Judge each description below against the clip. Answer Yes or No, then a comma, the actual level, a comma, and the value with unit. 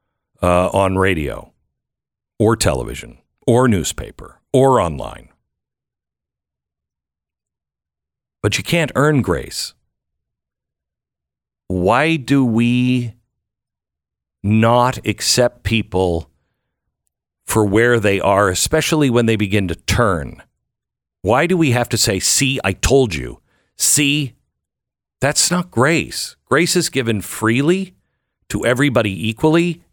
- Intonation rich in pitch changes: Yes, wide, 7.1 semitones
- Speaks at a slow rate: Yes, slow, 100 wpm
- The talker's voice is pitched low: Yes, low, 110 Hz